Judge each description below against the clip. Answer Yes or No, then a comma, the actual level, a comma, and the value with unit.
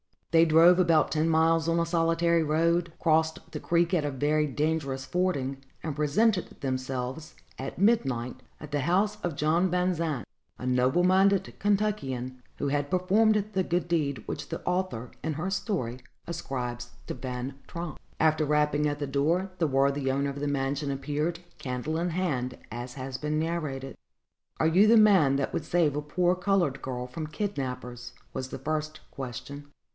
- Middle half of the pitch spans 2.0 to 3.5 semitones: No, average, 4.3 semitones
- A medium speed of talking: Yes, average, 170 wpm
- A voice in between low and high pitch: Yes, medium, 155 Hz